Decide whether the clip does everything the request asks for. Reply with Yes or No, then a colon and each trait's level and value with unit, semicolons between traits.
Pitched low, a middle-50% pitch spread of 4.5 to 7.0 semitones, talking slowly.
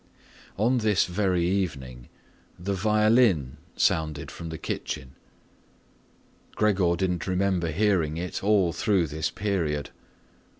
No: very low, 90 Hz; average, 4.1 semitones; slow, 110 wpm